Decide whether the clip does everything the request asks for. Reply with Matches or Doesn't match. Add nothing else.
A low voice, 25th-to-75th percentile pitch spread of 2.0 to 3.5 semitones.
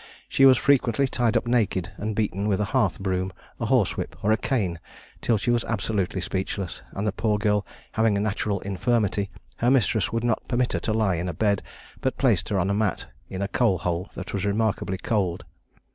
Matches